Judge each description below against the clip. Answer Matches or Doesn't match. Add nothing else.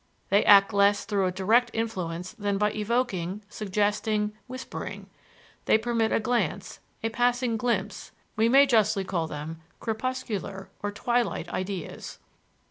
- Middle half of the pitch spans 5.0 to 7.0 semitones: Doesn't match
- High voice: Matches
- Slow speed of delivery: Matches